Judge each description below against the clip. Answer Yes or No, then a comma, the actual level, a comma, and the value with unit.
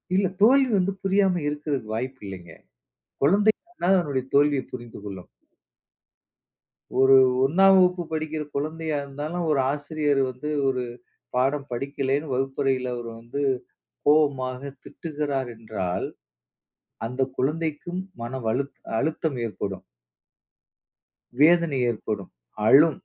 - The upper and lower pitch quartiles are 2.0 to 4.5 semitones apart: Yes, average, 3.9 semitones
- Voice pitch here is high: No, medium, 140 Hz